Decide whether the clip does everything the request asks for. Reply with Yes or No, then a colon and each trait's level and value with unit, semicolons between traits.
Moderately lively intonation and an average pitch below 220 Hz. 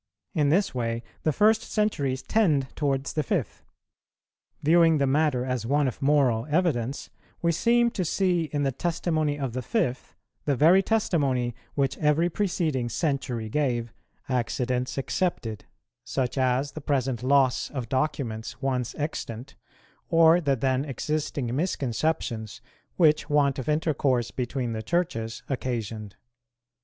Yes: average, 4.0 semitones; medium, 140 Hz